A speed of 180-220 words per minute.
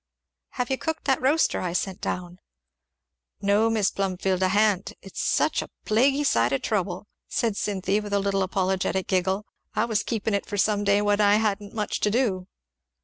Yes: average, 185 wpm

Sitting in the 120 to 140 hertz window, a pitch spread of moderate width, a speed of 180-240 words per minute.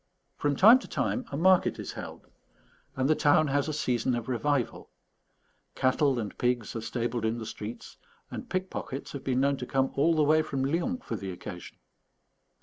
Yes: low, 135 Hz; average, 4.3 semitones; average, 185 wpm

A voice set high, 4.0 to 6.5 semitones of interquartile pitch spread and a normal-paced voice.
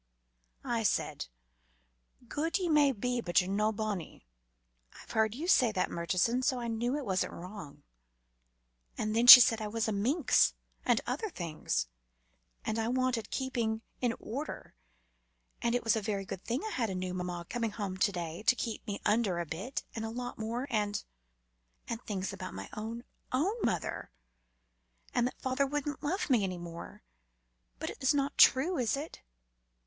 Yes: high, 225 Hz; average, 4.5 semitones; average, 175 wpm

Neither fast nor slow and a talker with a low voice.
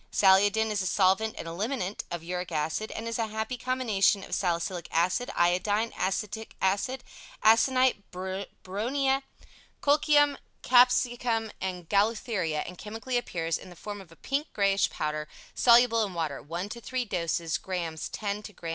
No: average, 155 wpm; high, 205 Hz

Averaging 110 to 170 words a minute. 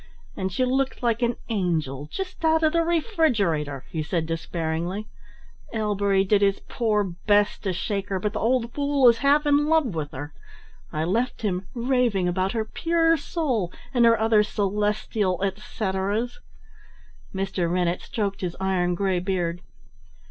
Yes: average, 155 wpm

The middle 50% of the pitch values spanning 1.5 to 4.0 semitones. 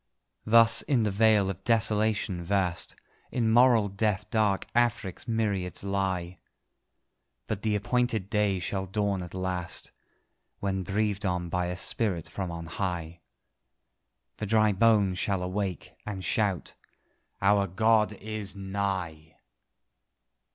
Yes: average, 2.7 semitones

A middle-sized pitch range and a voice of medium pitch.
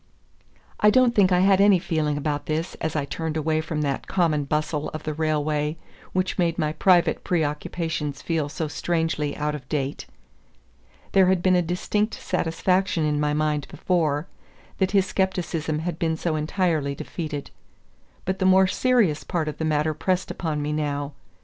Yes: average, 3.4 semitones; medium, 160 Hz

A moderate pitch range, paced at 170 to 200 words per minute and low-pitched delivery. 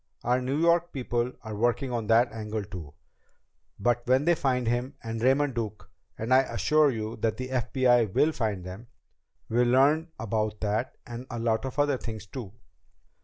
Yes: average, 3.1 semitones; average, 175 wpm; low, 120 Hz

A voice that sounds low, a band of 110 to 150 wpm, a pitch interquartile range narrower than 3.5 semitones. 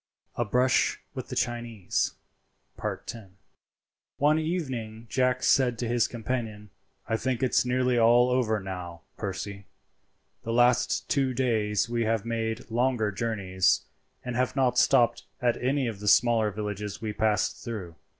Yes: low, 115 Hz; average, 140 wpm; average, 2.8 semitones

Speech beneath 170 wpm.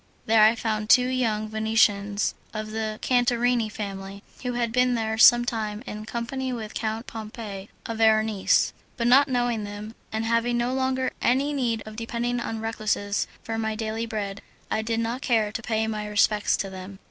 No: average, 180 wpm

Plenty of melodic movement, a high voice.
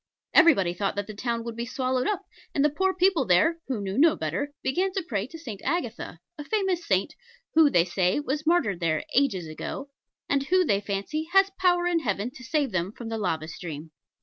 Yes: wide, 8.7 semitones; very high, 255 Hz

